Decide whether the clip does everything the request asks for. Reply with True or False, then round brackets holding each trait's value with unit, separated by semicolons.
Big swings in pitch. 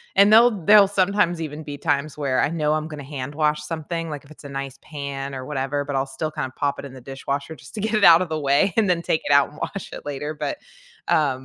False (3.2 semitones)